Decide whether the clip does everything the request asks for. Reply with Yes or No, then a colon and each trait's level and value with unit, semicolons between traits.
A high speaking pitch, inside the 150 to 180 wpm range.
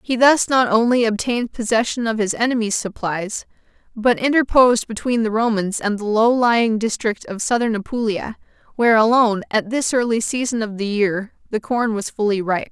Yes: high, 225 Hz; average, 175 wpm